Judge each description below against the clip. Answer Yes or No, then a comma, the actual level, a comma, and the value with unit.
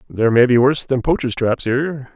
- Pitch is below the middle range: Yes, low, 125 Hz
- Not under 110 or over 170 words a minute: No, fast, 220 wpm